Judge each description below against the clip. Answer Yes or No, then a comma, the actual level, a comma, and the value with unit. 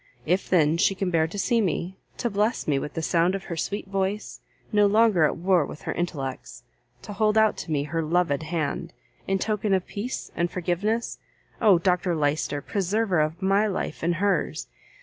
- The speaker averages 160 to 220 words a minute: Yes, average, 190 wpm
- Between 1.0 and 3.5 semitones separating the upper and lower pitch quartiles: No, average, 3.9 semitones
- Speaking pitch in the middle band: Yes, medium, 180 Hz